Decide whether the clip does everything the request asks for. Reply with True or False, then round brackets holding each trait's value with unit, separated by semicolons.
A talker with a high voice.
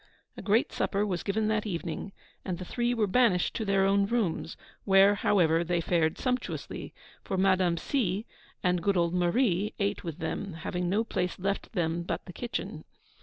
True (195 Hz)